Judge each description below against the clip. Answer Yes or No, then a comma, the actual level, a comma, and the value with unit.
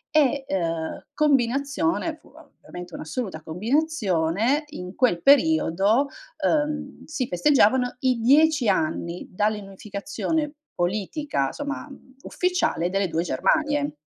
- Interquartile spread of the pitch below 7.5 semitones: No, wide, 8.4 semitones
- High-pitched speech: Yes, very high, 250 Hz